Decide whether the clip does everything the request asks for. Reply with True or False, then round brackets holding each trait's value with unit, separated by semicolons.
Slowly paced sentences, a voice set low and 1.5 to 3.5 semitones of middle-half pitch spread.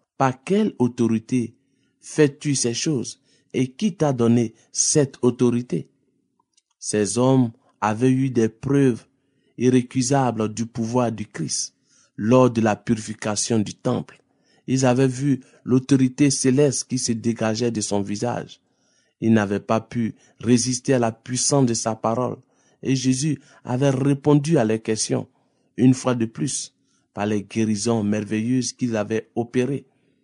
True (135 wpm; 125 Hz; 3.1 semitones)